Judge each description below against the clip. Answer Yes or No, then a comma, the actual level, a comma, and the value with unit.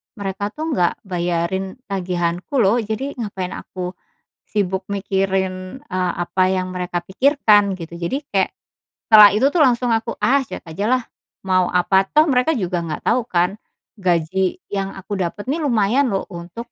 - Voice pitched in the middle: No, high, 195 Hz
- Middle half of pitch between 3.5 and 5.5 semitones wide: Yes, average, 4.3 semitones